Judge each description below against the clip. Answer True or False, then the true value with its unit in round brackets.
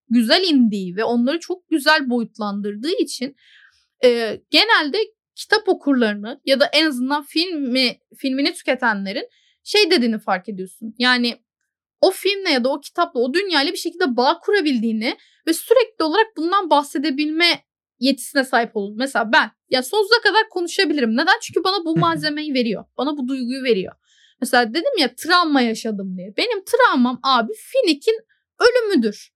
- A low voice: False (285 Hz)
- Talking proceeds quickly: True (145 wpm)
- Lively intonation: True (6.8 semitones)